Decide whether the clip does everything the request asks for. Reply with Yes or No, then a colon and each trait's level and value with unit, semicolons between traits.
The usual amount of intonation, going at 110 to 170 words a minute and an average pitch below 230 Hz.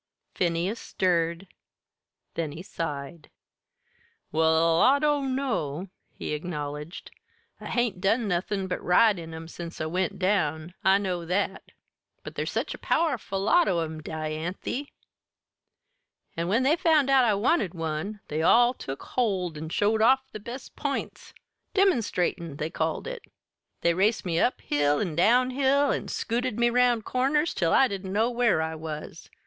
No: wide, 6.8 semitones; average, 155 wpm; high, 190 Hz